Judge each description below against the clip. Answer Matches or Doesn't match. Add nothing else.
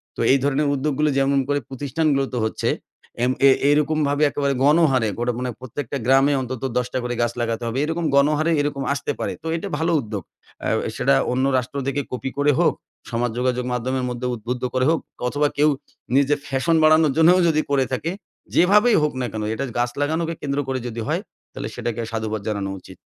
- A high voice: Doesn't match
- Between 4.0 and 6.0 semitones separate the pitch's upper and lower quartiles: Doesn't match